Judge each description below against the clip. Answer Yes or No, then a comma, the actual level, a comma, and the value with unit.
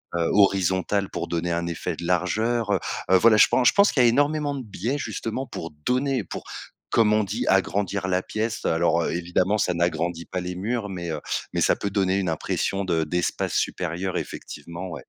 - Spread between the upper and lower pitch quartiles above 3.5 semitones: Yes, average, 4.2 semitones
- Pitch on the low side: Yes, very low, 95 Hz